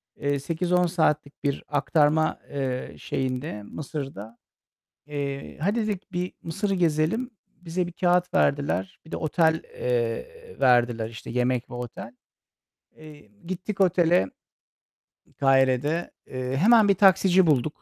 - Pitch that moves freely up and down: Yes, wide, 5.7 semitones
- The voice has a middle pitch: Yes, medium, 150 Hz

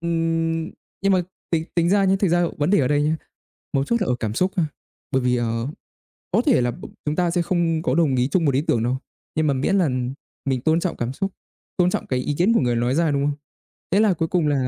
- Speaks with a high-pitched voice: No, medium, 160 Hz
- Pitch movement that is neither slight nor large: Yes, average, 4.9 semitones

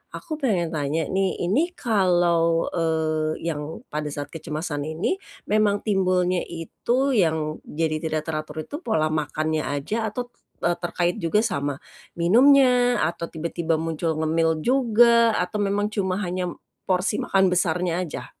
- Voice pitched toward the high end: No, medium, 175 Hz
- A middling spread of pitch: Yes, average, 4.6 semitones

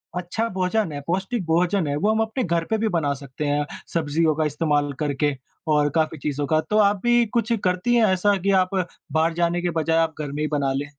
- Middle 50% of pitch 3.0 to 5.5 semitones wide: Yes, average, 5.0 semitones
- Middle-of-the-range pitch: Yes, medium, 165 Hz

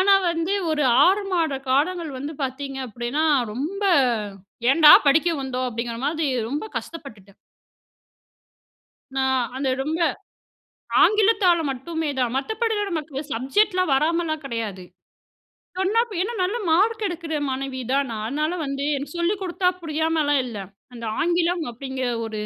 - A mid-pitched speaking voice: No, very high, 310 Hz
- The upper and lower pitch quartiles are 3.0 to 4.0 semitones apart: No, average, 4.9 semitones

